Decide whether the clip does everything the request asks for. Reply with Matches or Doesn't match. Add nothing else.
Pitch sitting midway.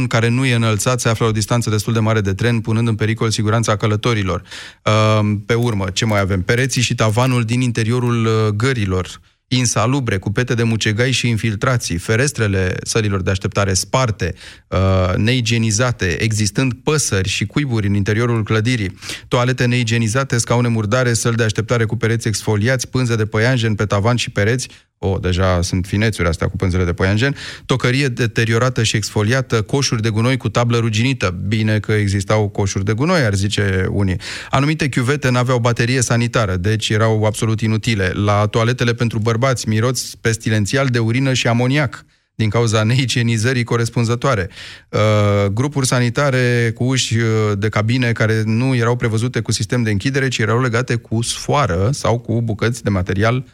Doesn't match